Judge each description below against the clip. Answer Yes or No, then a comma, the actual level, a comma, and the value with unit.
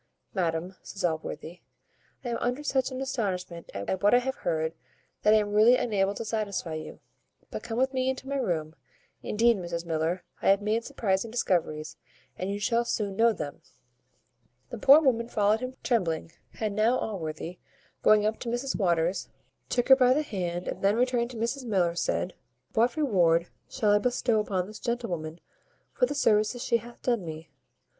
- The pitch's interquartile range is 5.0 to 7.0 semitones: Yes, wide, 5.5 semitones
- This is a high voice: Yes, high, 210 Hz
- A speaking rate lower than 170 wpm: No, average, 180 wpm